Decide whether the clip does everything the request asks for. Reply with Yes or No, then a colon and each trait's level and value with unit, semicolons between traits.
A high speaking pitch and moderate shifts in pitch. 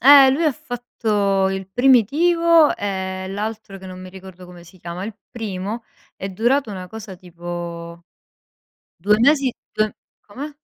Yes: high, 205 Hz; average, 4.8 semitones